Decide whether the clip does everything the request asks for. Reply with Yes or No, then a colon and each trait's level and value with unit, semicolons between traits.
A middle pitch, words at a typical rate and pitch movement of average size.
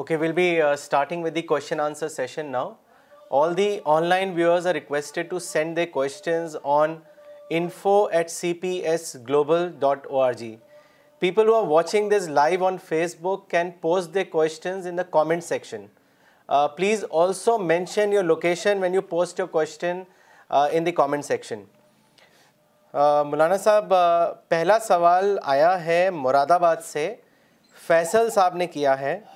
Yes: medium, 170 Hz; average, 155 wpm; average, 3.5 semitones